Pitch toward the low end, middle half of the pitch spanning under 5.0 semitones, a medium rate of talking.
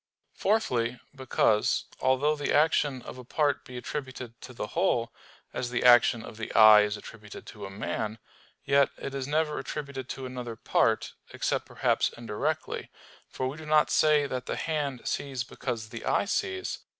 Yes: low, 130 Hz; average, 4.1 semitones; average, 170 wpm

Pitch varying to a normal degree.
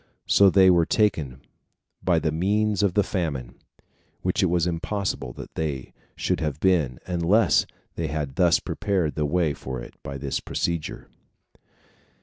Yes: average, 4.3 semitones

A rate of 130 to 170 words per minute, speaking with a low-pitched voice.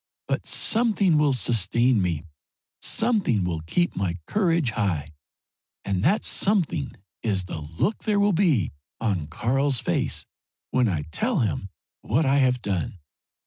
Yes: average, 140 wpm; low, 120 Hz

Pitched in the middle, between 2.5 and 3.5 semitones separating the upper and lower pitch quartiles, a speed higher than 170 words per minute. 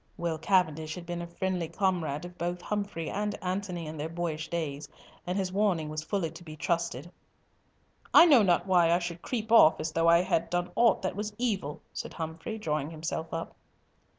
Yes: medium, 170 Hz; average, 2.8 semitones; average, 195 wpm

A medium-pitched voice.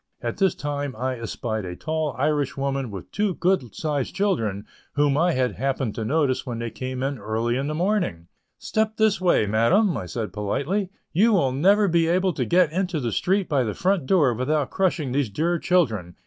Yes: medium, 145 Hz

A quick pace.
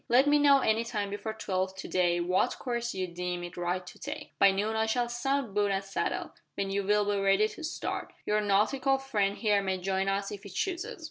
Yes: fast, 225 wpm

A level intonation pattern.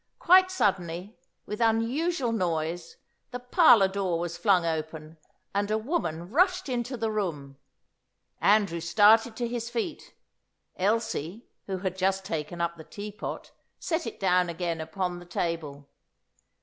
No: average, 5.2 semitones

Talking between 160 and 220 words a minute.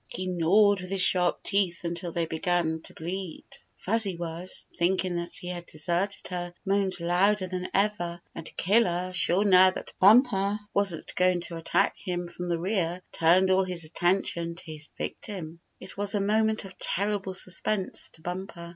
Yes: average, 175 wpm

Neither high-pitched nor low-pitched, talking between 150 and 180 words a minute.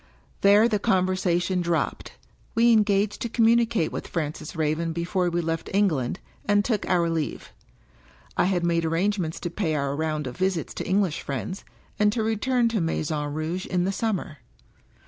Yes: medium, 180 Hz; average, 165 wpm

